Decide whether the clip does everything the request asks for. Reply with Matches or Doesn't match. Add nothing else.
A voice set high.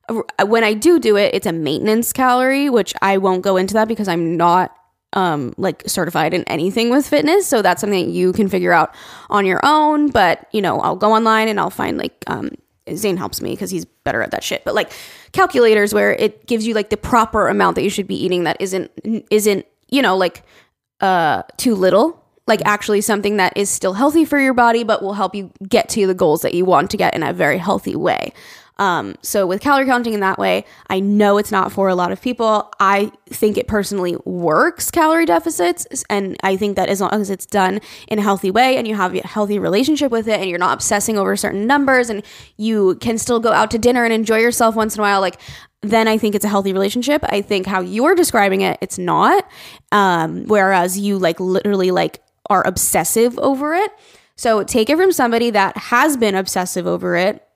Matches